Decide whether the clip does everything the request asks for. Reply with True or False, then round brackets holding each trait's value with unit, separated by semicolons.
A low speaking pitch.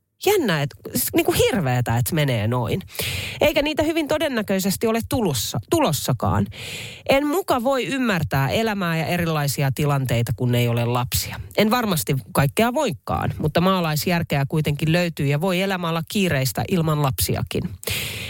False (155 Hz)